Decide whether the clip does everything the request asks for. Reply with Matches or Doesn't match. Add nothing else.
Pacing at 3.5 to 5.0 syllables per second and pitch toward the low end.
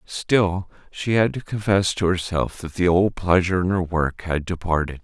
Matches